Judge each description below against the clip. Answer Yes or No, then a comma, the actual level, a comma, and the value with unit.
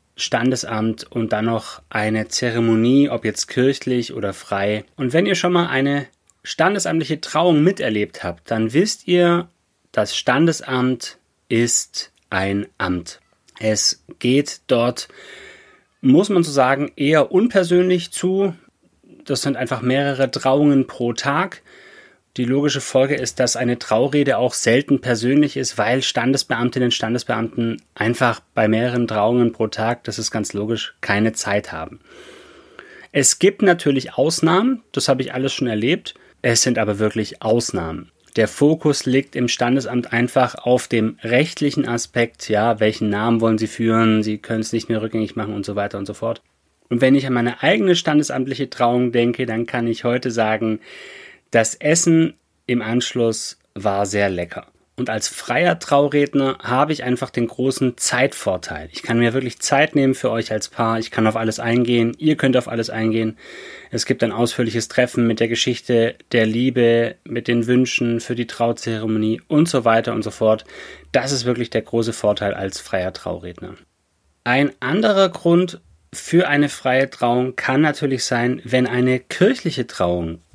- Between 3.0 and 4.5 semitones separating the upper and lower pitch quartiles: Yes, average, 3.7 semitones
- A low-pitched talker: Yes, low, 120 Hz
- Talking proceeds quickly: No, average, 160 wpm